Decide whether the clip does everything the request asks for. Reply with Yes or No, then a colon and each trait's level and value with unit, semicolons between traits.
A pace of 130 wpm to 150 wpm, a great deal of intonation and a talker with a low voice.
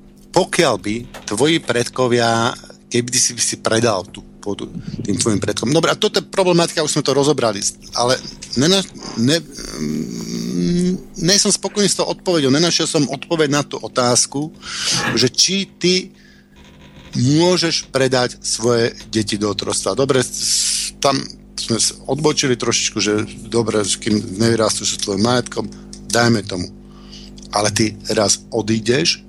Yes: average, 135 wpm; wide, 6.2 semitones; low, 120 Hz